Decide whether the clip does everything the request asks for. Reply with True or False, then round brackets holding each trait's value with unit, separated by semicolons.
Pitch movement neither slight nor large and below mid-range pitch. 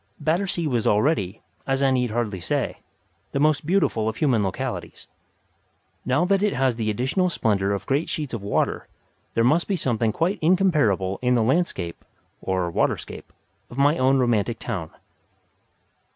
False (6.3 semitones; 125 Hz)